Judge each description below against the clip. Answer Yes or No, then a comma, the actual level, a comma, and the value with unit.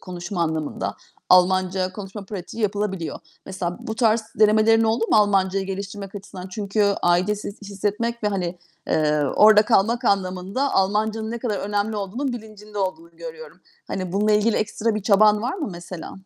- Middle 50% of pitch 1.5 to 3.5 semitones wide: Yes, narrow, 2.5 semitones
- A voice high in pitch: Yes, high, 205 Hz